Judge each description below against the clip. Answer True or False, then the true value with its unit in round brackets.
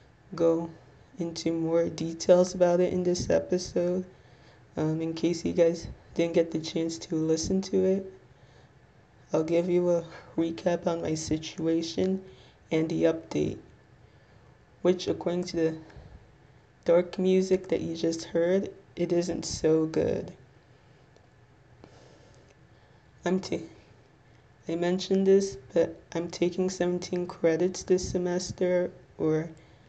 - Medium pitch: True (165 Hz)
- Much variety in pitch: False (3.9 semitones)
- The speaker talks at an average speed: False (120 wpm)